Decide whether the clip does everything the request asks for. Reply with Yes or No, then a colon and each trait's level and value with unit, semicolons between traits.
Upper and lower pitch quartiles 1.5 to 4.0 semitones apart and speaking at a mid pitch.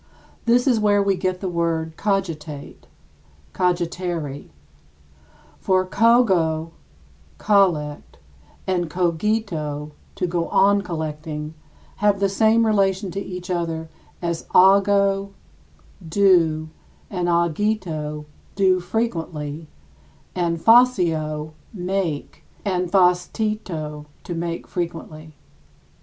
Yes: average, 3.7 semitones; medium, 180 Hz